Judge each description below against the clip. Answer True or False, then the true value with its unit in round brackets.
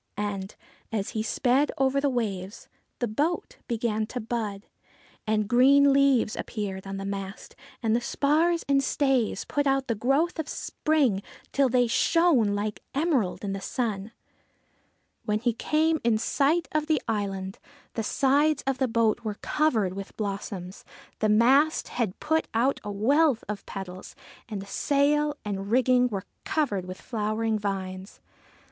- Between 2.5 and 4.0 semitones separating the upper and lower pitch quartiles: False (5.4 semitones)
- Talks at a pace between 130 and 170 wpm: True (155 wpm)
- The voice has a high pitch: True (230 Hz)